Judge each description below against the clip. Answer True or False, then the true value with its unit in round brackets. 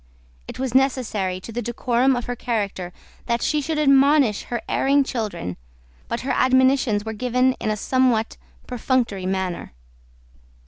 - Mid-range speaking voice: False (245 Hz)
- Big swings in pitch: False (3.5 semitones)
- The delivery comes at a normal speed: True (145 wpm)